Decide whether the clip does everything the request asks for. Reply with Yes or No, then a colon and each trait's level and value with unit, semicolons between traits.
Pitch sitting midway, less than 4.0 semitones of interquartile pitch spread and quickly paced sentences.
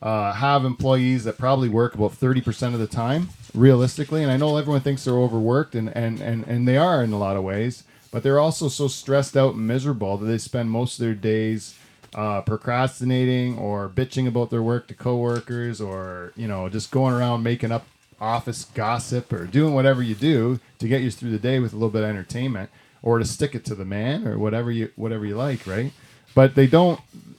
No: low, 120 Hz; average, 2.9 semitones; fast, 215 wpm